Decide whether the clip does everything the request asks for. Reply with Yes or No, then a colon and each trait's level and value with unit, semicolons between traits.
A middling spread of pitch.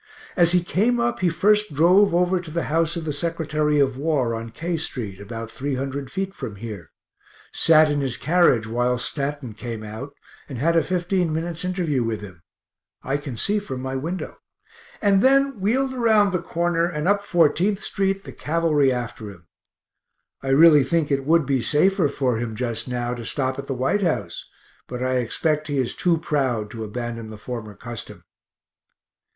No: wide, 6.0 semitones